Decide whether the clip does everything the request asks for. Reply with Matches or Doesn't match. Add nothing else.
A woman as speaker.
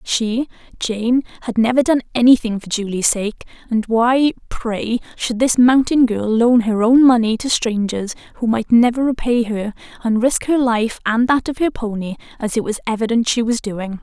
Matches